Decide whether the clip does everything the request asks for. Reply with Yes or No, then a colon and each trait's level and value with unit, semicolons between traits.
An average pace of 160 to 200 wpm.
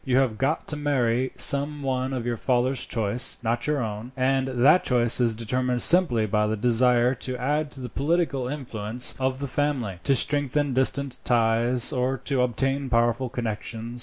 Yes: average, 175 wpm